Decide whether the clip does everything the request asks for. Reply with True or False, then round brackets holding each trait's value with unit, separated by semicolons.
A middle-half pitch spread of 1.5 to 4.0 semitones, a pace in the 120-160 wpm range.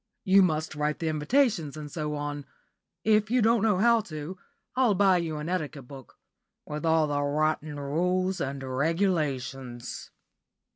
False (4.5 semitones; 150 wpm)